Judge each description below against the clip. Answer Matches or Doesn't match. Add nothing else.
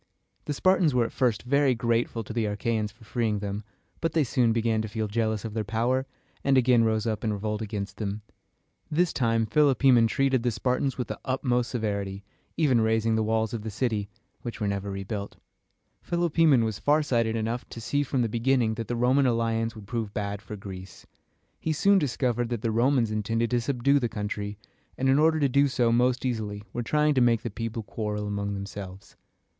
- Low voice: Matches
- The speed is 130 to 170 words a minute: Doesn't match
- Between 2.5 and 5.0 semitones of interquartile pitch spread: Matches